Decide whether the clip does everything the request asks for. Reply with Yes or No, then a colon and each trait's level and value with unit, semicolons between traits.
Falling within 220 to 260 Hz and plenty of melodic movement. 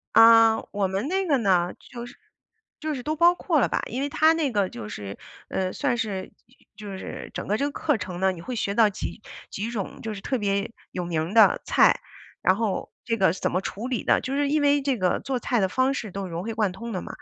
Yes: high, 225 Hz; wide, 5.7 semitones